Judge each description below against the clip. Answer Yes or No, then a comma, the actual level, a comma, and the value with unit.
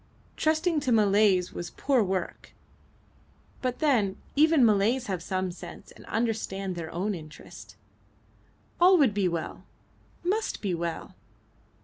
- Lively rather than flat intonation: Yes, wide, 6.2 semitones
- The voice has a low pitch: No, high, 205 Hz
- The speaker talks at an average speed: No, slow, 125 wpm